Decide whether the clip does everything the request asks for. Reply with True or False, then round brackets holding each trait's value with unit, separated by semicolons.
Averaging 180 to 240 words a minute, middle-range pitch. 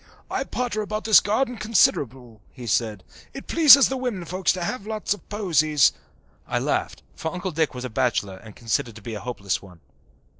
True (190 wpm; 165 Hz)